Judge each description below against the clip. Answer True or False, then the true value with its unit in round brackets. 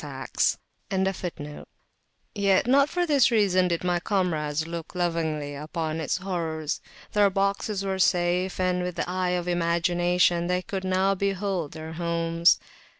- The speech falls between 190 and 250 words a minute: False (140 wpm)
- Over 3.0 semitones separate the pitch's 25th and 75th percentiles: False (2.4 semitones)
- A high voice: False (180 Hz)